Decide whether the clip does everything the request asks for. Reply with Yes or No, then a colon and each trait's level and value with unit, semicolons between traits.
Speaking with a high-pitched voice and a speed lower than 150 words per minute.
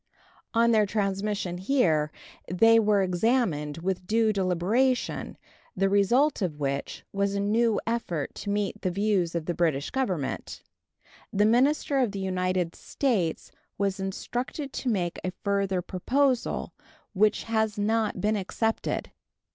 Yes: high, 200 Hz; slow, 135 wpm